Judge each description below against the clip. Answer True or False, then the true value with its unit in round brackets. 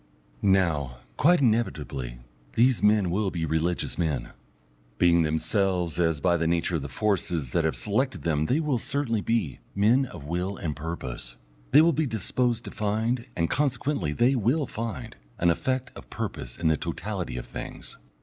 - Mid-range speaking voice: False (95 Hz)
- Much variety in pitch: True (6.8 semitones)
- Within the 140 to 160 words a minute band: False (170 wpm)